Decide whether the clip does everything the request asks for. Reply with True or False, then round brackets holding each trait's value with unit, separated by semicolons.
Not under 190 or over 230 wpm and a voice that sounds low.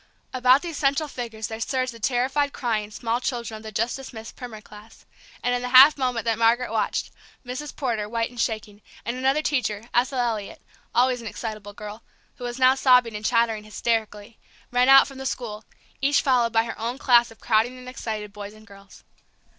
False (195 wpm; 235 Hz)